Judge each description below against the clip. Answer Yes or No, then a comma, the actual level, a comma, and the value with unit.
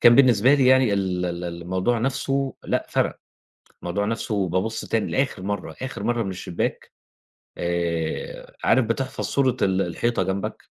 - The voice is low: Yes, low, 105 Hz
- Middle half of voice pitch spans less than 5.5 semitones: No, wide, 5.9 semitones